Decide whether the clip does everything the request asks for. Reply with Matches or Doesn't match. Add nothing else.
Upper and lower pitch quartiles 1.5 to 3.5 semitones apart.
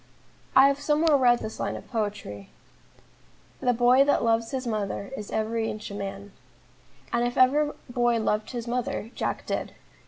Matches